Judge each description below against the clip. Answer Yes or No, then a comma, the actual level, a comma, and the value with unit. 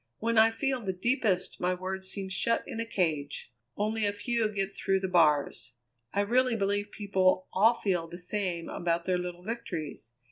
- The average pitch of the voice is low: No, high, 195 Hz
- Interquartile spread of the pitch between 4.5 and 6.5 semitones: No, average, 3.7 semitones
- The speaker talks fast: No, average, 180 wpm